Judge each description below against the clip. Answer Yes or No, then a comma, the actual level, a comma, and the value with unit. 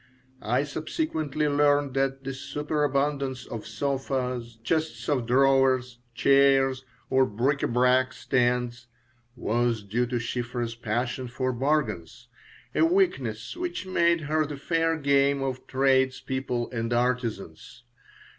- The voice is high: No, low, 130 Hz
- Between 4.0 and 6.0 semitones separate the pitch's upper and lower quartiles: No, average, 2.9 semitones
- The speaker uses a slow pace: Yes, slow, 120 wpm